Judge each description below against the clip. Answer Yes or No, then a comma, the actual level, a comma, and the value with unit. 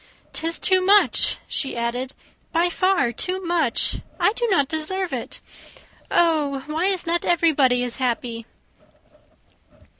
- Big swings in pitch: Yes, wide, 6.0 semitones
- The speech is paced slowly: Yes, slow, 125 wpm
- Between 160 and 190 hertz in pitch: No, very high, 320 Hz